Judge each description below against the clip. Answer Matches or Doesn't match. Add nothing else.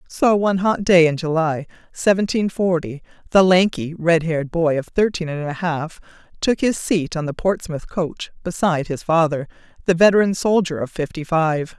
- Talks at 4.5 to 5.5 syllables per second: Matches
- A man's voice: Doesn't match